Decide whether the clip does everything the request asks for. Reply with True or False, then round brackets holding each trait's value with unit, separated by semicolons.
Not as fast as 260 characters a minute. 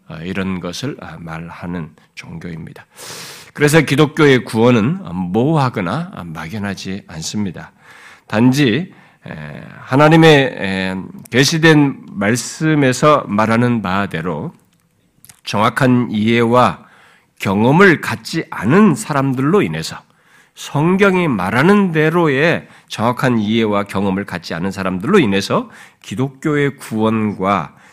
True (235 characters per minute)